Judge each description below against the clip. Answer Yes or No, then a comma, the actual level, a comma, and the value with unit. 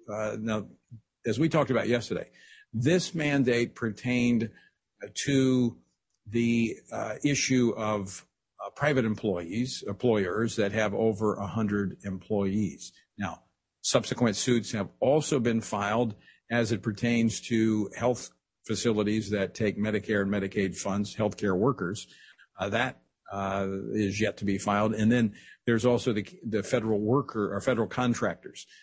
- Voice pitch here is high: No, low, 110 Hz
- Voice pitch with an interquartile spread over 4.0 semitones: No, average, 2.7 semitones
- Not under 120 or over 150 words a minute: Yes, slow, 135 wpm